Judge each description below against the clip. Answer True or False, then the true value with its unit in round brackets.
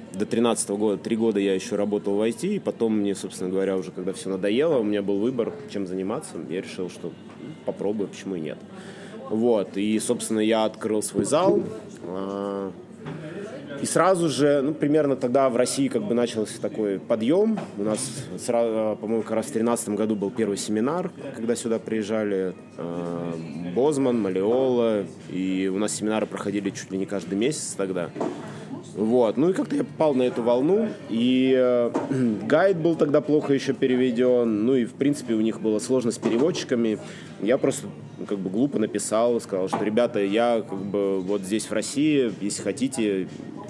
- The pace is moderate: False (170 wpm)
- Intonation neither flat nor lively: True (3.8 semitones)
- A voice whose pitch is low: True (110 Hz)